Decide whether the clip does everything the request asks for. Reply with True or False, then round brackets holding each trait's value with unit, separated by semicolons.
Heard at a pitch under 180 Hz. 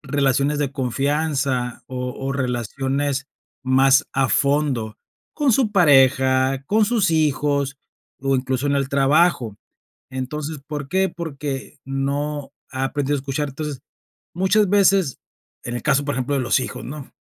True (140 Hz)